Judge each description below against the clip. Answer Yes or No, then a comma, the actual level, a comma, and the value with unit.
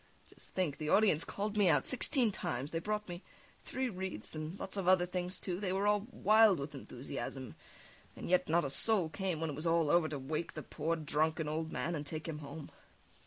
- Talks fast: Yes, fast, 215 wpm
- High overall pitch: No, medium, 170 Hz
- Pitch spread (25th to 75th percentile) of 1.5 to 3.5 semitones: No, average, 4.0 semitones